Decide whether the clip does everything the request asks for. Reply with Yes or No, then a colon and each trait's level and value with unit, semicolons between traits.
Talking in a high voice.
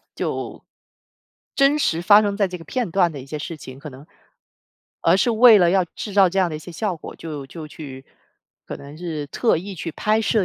No: medium, 175 Hz